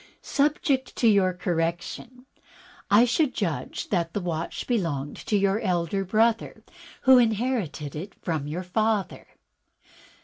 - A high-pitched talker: Yes, high, 195 Hz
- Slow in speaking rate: Yes, slow, 125 wpm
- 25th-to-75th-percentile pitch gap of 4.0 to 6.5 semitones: Yes, wide, 5.5 semitones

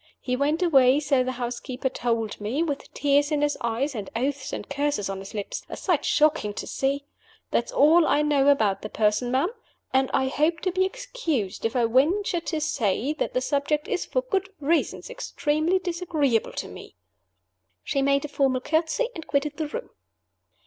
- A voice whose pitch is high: Yes, very high, 285 Hz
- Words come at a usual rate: Yes, average, 185 wpm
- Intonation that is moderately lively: Yes, average, 4.1 semitones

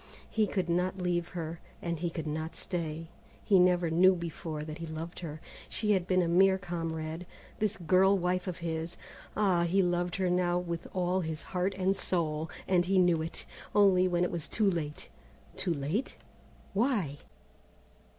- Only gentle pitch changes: Yes, narrow, 2.2 semitones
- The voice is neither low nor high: Yes, medium, 175 Hz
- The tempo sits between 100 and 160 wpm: No, average, 175 wpm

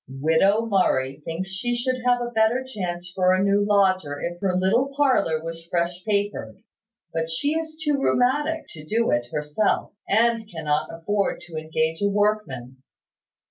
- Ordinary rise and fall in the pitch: No, wide, 6.1 semitones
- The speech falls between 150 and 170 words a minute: Yes, average, 160 wpm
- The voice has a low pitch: No, high, 190 Hz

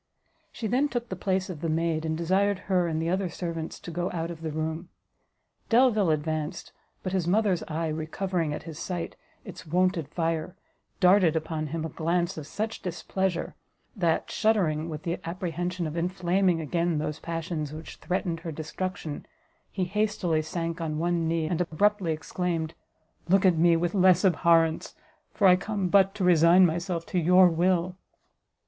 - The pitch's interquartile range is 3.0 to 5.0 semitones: No, narrow, 2.5 semitones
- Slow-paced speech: No, average, 170 wpm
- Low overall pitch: No, medium, 170 Hz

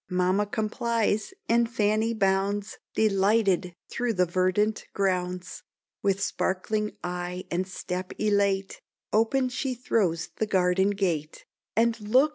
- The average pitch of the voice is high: Yes, high, 200 Hz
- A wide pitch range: No, average, 3.1 semitones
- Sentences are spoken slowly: Yes, slow, 115 wpm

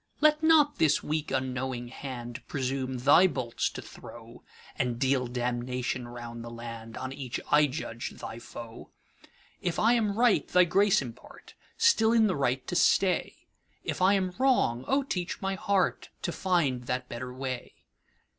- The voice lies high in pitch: No, low, 135 Hz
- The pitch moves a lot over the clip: Yes, wide, 7.4 semitones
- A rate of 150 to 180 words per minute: No, slow, 135 wpm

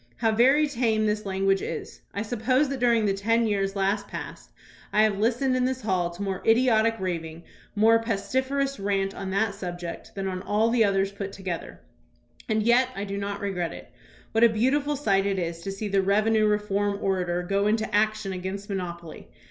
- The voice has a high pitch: Yes, high, 205 Hz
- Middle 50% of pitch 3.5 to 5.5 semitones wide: No, average, 2.7 semitones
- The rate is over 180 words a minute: Yes, average, 195 wpm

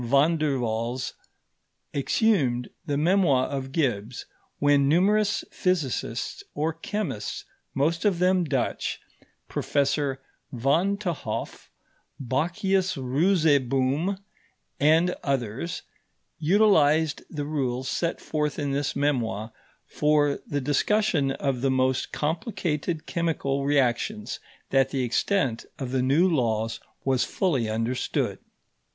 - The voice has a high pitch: No, medium, 145 Hz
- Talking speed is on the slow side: Yes, slow, 105 wpm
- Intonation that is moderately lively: Yes, average, 4.4 semitones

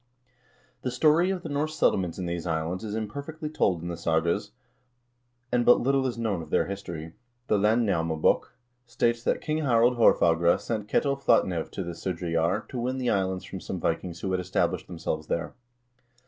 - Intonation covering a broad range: Yes, wide, 6.4 semitones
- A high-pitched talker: No, low, 100 Hz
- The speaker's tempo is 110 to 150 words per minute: No, average, 180 wpm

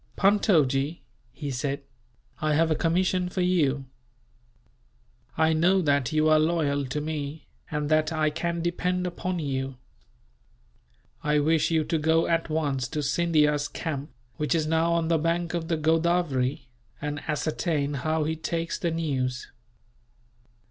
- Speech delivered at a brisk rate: No, average, 145 wpm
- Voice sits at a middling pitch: Yes, medium, 155 Hz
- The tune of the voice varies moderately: No, narrow, 2.3 semitones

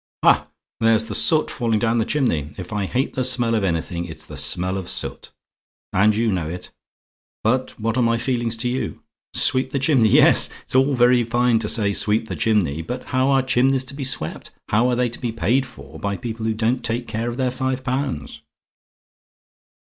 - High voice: No, low, 115 Hz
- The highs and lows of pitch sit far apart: No, average, 3.4 semitones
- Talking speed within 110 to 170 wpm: No, fast, 205 wpm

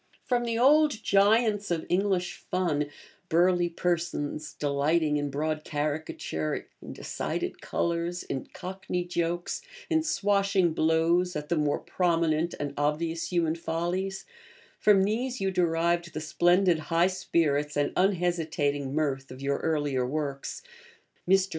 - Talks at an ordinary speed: No, slow, 130 wpm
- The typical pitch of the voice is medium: Yes, medium, 170 Hz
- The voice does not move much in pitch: No, average, 3.7 semitones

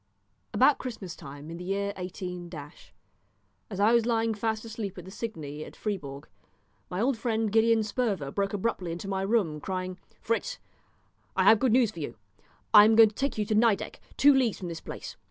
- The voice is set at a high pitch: Yes, high, 205 Hz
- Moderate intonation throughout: Yes, average, 4.1 semitones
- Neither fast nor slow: Yes, average, 190 wpm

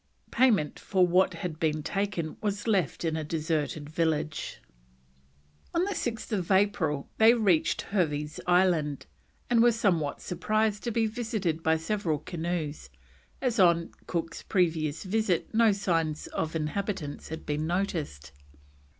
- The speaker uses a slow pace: Yes, slow, 130 wpm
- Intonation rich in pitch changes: No, average, 4.7 semitones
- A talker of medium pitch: Yes, medium, 175 Hz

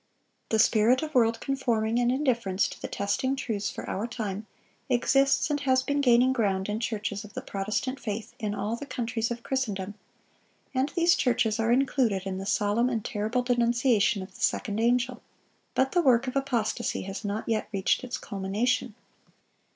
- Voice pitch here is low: No, high, 235 Hz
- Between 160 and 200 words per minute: Yes, average, 175 wpm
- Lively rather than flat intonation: No, average, 3.7 semitones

